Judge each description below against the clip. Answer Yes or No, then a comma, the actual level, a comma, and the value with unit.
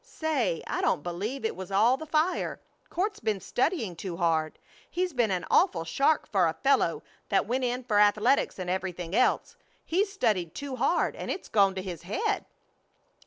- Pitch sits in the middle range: No, high, 215 Hz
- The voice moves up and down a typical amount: No, wide, 7.6 semitones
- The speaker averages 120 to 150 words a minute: No, average, 180 wpm